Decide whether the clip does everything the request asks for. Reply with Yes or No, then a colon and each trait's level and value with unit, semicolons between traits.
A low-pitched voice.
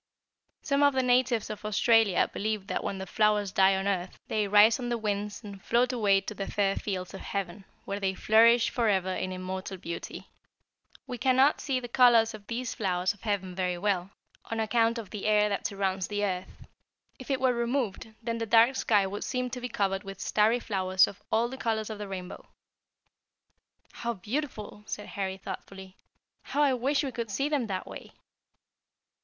No: high, 210 Hz